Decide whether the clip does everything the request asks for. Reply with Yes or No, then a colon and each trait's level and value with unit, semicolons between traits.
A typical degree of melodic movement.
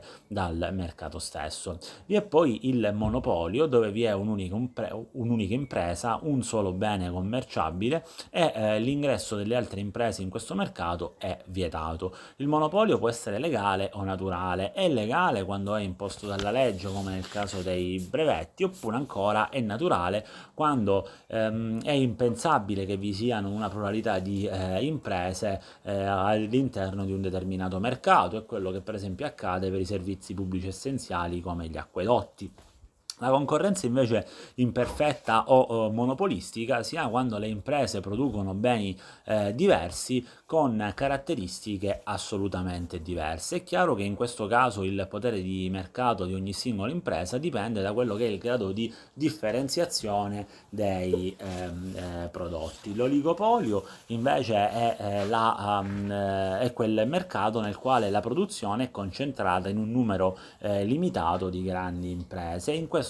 Yes: average, 4.4 semitones